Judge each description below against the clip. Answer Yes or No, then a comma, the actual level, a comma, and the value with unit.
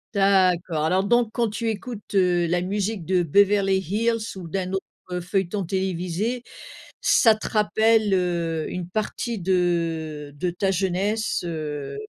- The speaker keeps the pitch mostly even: No, average, 3.3 semitones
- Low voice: No, high, 190 Hz